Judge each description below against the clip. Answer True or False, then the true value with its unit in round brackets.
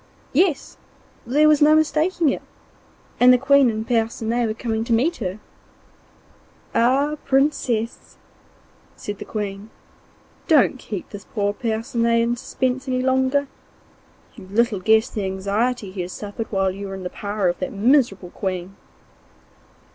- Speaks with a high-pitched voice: True (230 Hz)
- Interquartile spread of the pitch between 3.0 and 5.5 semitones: True (4.5 semitones)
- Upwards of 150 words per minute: False (145 wpm)